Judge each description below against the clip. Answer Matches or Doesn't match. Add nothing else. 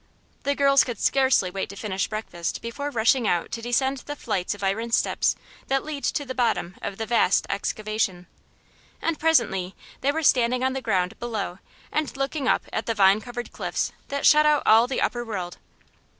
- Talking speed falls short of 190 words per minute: Doesn't match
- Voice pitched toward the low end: Doesn't match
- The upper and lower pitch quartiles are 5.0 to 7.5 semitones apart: Matches